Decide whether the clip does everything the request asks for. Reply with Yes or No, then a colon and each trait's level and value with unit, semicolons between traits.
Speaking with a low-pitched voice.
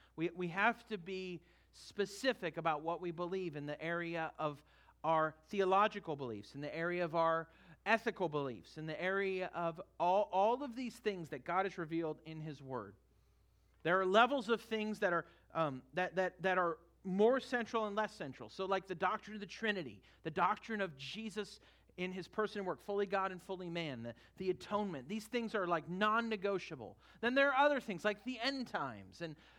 No: medium, 185 Hz